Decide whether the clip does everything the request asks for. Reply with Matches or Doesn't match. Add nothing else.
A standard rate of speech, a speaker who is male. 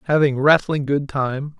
Matches